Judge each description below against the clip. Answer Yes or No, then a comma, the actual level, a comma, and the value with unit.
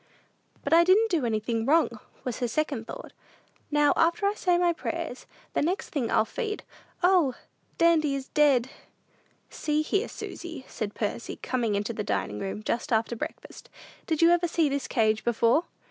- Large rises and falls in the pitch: Yes, wide, 6.5 semitones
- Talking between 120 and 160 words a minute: No, average, 170 wpm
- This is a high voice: Yes, very high, 290 Hz